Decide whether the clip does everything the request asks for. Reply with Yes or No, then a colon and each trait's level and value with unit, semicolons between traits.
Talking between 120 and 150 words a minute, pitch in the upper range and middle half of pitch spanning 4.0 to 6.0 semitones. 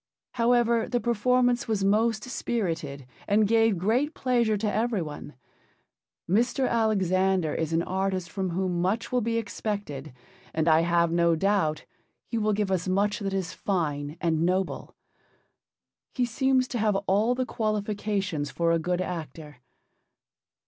Yes: average, 145 wpm; high, 200 Hz; average, 4.9 semitones